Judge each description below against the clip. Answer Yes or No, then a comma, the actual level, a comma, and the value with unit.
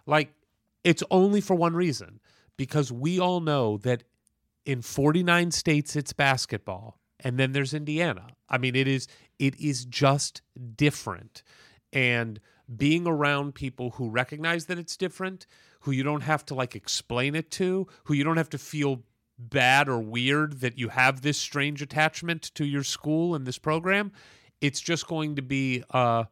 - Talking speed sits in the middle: Yes, average, 165 wpm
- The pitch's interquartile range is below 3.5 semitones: No, average, 3.9 semitones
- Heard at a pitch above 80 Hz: Yes, medium, 140 Hz